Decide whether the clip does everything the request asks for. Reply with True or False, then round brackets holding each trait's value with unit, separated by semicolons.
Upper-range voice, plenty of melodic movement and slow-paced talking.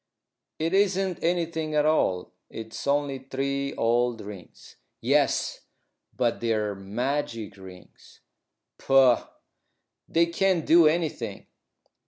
False (140 Hz; 6.2 semitones; 100 wpm)